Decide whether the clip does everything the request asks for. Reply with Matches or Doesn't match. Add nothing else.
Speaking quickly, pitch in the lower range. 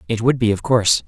Matches